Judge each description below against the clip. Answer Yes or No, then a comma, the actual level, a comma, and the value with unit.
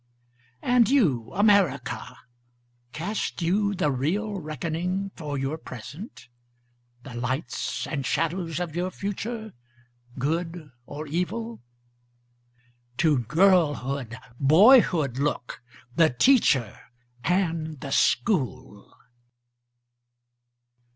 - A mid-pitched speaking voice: Yes, medium, 160 Hz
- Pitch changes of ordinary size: No, wide, 5.9 semitones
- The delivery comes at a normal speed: No, slow, 85 wpm